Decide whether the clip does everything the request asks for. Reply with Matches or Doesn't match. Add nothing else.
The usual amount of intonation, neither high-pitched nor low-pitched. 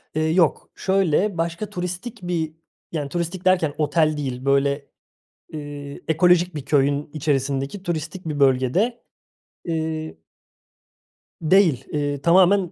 Matches